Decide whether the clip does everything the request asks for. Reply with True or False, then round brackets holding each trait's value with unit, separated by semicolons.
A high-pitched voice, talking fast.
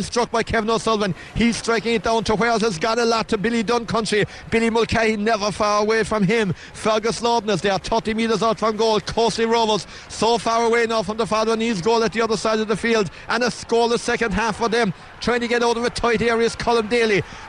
True (225 Hz; 235 wpm)